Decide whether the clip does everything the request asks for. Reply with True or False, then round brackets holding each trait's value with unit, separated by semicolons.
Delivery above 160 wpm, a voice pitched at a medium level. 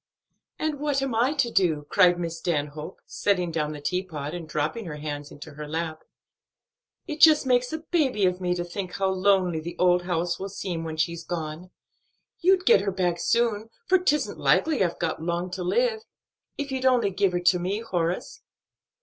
True (190 wpm; 180 Hz)